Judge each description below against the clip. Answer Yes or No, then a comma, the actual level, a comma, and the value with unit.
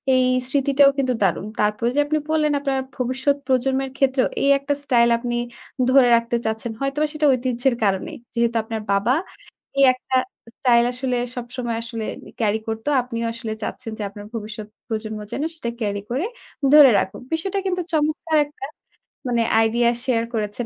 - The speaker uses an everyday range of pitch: Yes, average, 3.3 semitones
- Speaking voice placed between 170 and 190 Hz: No, high, 245 Hz